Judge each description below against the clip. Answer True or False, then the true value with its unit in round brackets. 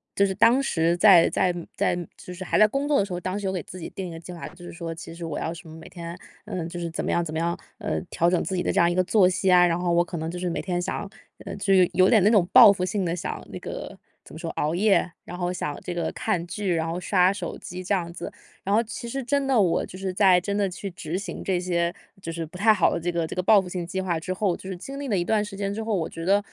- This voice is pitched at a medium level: True (180 Hz)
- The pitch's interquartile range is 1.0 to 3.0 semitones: True (2.7 semitones)